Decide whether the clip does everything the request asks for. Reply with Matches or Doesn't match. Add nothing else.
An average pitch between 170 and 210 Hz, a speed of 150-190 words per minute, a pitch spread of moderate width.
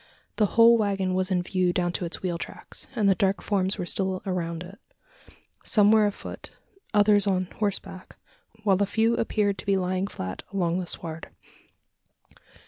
Doesn't match